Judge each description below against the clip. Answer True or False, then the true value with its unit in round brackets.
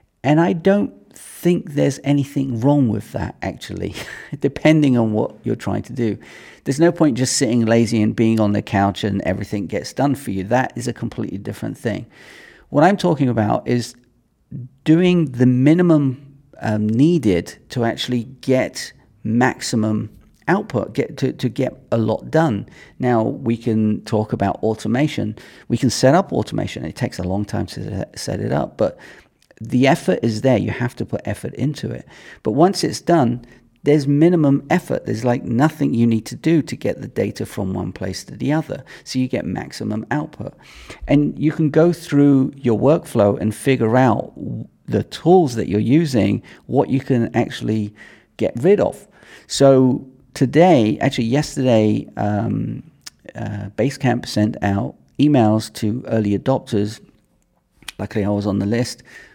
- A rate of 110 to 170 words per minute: True (165 wpm)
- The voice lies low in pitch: True (120 Hz)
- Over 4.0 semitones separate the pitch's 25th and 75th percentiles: True (4.7 semitones)